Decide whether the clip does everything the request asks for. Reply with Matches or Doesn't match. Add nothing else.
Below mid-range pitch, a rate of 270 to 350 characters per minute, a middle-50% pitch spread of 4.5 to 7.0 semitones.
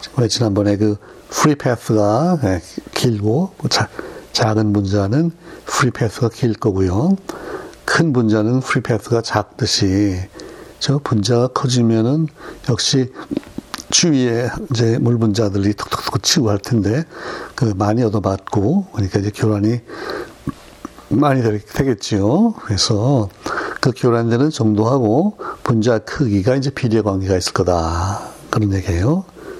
Doesn't match